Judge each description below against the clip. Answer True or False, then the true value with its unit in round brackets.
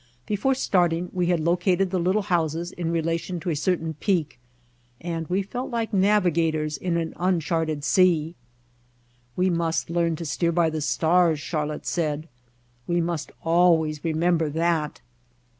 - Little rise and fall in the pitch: True (2.0 semitones)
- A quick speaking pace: False (155 wpm)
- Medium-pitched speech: True (170 Hz)